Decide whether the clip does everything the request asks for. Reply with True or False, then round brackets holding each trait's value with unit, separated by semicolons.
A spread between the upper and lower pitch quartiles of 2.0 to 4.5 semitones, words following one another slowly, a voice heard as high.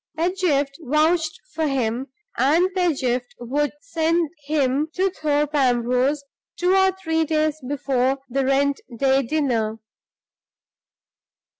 True (3.4 semitones; 110 wpm; 290 Hz)